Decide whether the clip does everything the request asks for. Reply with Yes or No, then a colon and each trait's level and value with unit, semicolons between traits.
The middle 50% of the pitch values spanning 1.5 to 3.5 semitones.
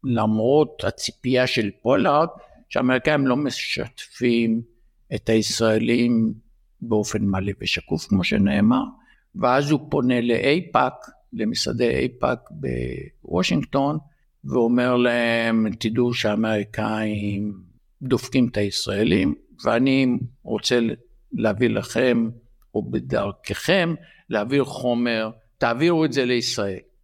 Yes: average, 2.9 semitones